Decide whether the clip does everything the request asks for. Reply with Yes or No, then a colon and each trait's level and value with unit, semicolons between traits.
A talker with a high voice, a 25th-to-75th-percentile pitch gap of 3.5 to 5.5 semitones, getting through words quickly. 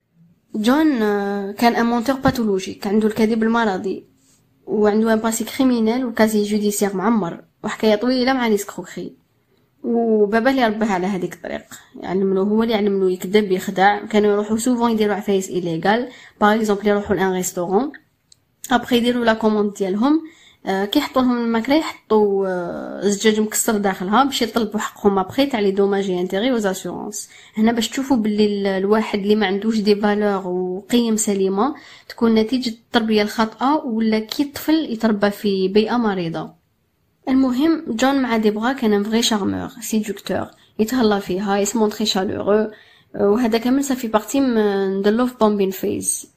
No: high, 215 Hz; average, 2.9 semitones; fast, 140 wpm